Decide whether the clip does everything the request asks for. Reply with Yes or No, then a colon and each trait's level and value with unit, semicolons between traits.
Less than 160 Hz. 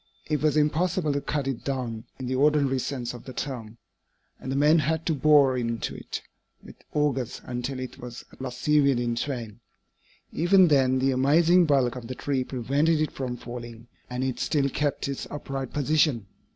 Yes: low, 135 Hz